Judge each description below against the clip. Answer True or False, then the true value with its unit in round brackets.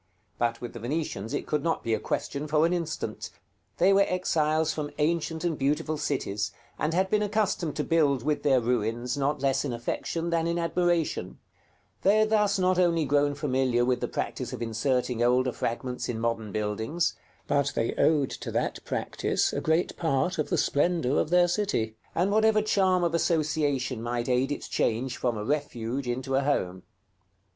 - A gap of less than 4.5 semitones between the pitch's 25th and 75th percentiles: False (5.5 semitones)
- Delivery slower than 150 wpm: False (185 wpm)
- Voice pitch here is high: False (145 Hz)